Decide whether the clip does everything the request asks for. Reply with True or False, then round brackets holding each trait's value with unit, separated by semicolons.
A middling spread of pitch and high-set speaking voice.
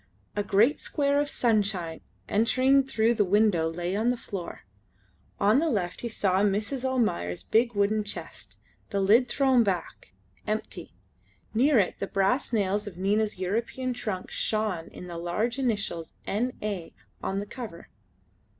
True (3.9 semitones; 210 Hz)